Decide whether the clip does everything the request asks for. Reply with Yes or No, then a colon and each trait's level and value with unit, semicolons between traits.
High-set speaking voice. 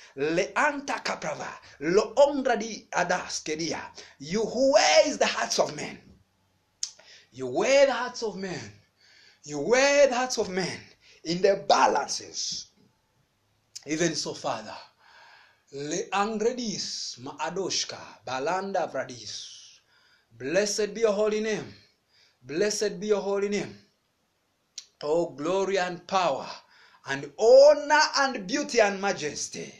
Yes: high, 205 Hz